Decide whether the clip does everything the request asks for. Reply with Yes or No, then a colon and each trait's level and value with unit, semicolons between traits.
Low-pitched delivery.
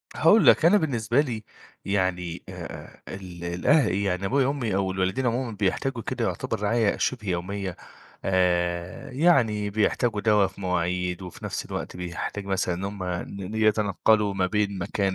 Yes: low, 100 Hz